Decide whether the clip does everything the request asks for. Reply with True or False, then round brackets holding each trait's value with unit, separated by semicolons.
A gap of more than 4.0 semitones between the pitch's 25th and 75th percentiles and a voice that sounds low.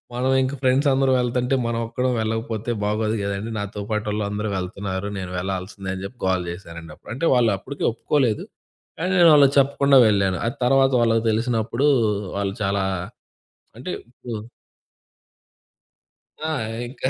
True (4.5 semitones; 115 Hz)